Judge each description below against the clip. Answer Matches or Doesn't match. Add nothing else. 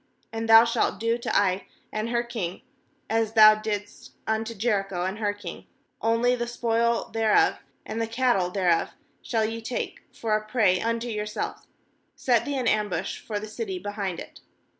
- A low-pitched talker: Doesn't match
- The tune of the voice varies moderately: Doesn't match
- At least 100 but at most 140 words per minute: Doesn't match